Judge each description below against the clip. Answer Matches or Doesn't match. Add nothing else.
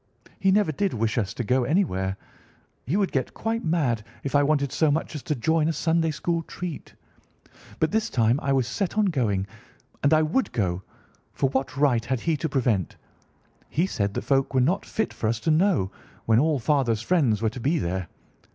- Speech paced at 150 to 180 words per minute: Doesn't match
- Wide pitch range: Matches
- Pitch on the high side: Doesn't match